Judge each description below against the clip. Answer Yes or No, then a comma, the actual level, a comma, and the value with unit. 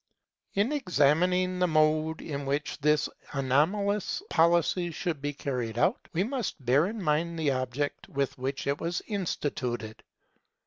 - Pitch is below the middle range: No, medium, 155 Hz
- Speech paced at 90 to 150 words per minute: Yes, average, 140 wpm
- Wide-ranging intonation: No, average, 4.6 semitones